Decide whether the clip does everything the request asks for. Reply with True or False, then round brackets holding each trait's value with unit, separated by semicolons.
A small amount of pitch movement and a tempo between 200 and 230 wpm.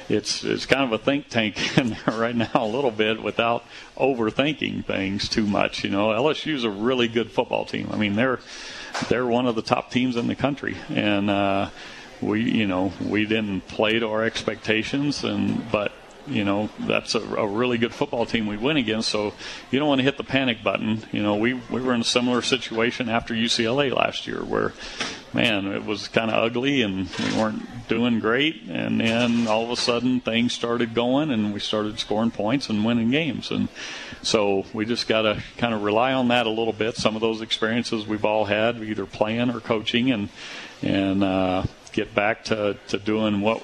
True (2.3 semitones; 205 wpm)